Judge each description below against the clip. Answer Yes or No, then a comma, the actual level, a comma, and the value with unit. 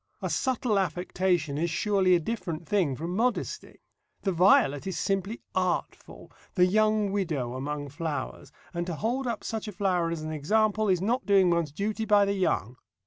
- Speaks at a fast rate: No, average, 175 wpm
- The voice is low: No, medium, 185 Hz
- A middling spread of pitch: Yes, average, 4.2 semitones